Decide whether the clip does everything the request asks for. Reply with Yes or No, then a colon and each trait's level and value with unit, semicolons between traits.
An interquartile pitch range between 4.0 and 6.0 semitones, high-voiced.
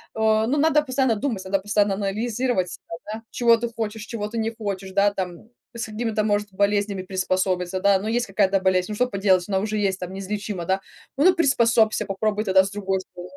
No: average, 2.8 semitones; high, 205 Hz